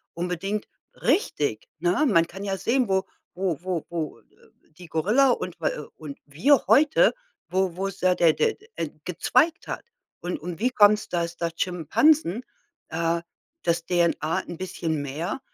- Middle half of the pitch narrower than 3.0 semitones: No, average, 3.8 semitones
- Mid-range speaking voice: Yes, medium, 180 Hz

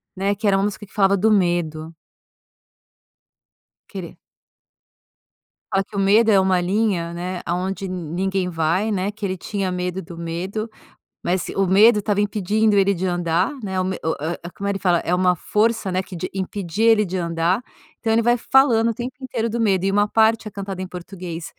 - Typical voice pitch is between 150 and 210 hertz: Yes, high, 195 Hz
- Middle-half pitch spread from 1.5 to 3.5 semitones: Yes, average, 2.7 semitones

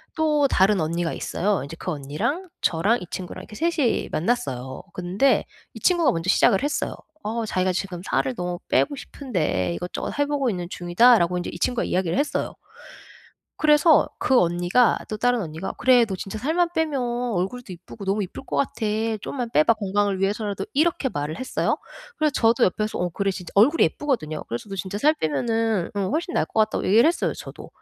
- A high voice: Yes, high, 205 Hz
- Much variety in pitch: Yes, wide, 6.6 semitones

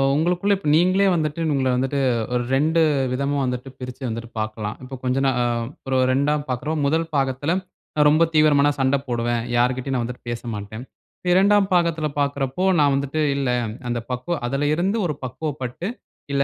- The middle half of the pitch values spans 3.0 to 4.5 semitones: Yes, average, 3.7 semitones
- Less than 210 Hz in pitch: Yes, medium, 140 Hz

